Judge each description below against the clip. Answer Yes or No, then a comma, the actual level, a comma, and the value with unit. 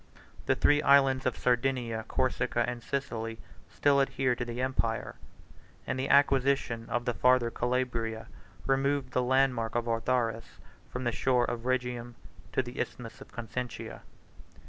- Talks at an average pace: Yes, average, 145 wpm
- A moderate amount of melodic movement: No, narrow, 1.9 semitones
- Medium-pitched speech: No, low, 125 Hz